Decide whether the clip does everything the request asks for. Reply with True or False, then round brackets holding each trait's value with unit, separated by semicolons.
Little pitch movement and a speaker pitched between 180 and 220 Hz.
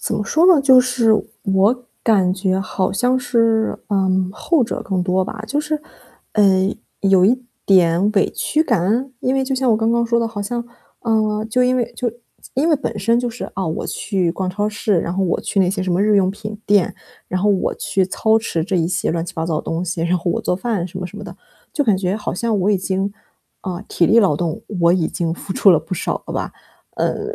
False (4.0 semitones; 200 Hz)